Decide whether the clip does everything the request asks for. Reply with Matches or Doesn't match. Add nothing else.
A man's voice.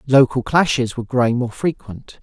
Matches